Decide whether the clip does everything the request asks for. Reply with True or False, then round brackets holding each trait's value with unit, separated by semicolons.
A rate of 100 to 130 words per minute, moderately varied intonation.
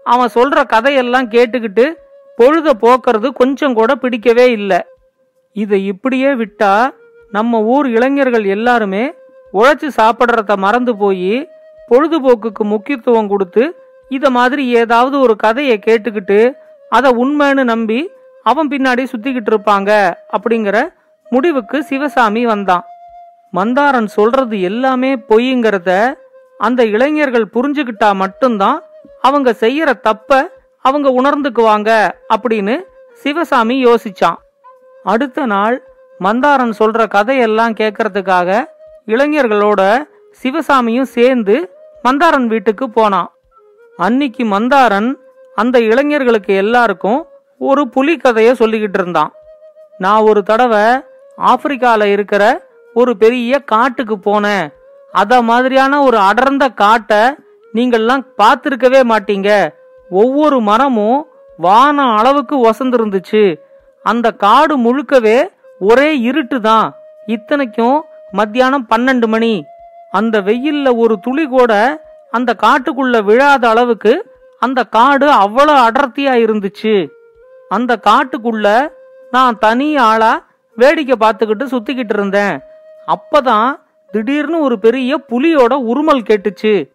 False (85 wpm; 4.1 semitones)